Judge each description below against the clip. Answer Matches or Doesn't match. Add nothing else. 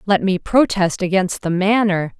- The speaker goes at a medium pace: Matches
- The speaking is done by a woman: Matches